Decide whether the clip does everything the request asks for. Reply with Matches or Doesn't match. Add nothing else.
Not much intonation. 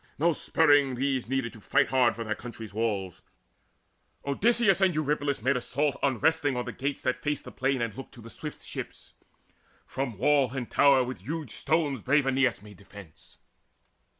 Doesn't match